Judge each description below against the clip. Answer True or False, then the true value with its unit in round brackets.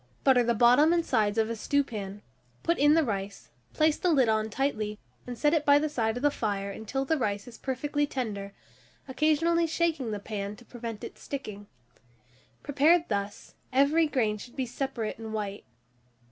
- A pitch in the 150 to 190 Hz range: False (245 Hz)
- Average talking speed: True (180 wpm)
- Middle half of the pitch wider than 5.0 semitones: True (5.5 semitones)